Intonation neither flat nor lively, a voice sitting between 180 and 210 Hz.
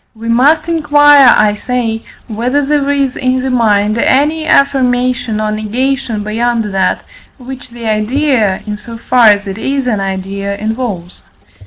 No: average, 4.0 semitones; high, 240 Hz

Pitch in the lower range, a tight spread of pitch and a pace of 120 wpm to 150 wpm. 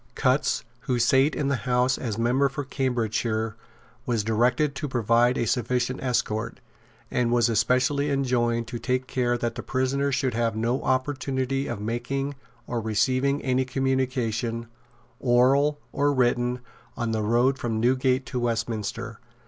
Yes: low, 125 Hz; narrow, 2.2 semitones; average, 145 wpm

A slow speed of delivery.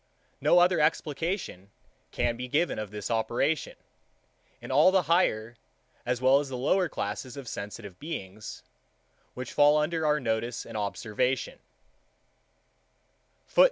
Yes: slow, 120 wpm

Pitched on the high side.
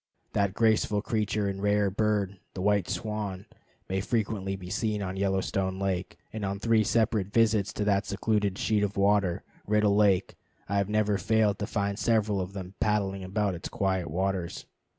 No: low, 100 Hz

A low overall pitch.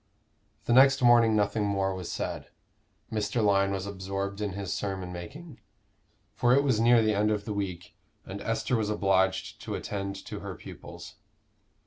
Yes: low, 100 Hz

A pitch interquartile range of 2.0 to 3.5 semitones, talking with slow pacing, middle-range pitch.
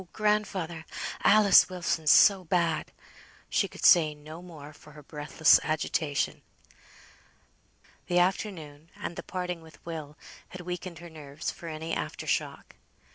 Yes: average, 2.8 semitones; slow, 130 wpm; medium, 165 Hz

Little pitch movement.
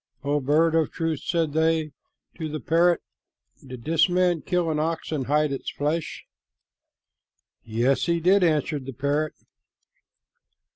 Yes: narrow, 2.3 semitones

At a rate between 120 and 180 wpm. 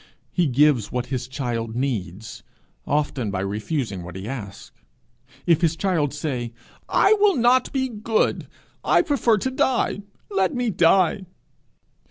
Yes: average, 140 wpm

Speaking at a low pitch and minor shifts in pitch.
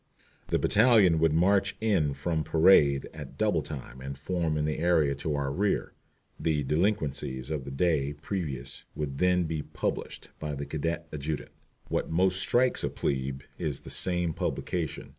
No: very low, 80 Hz; average, 4.0 semitones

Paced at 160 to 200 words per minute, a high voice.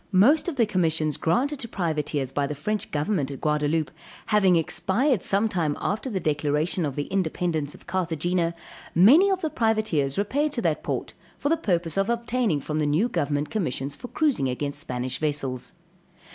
No: average, 175 wpm; medium, 170 Hz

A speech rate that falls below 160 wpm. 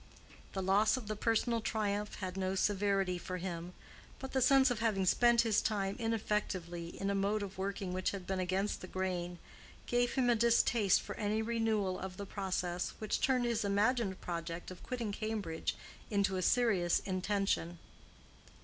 No: average, 170 wpm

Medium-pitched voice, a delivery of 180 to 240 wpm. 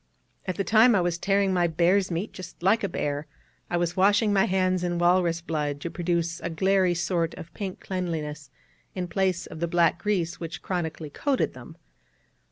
Yes: medium, 175 Hz; average, 185 wpm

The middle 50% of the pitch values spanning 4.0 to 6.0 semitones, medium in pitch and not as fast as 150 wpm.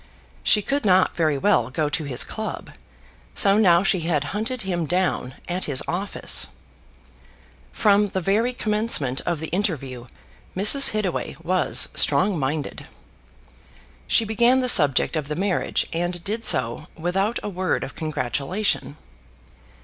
Yes: wide, 5.4 semitones; medium, 180 Hz; average, 140 wpm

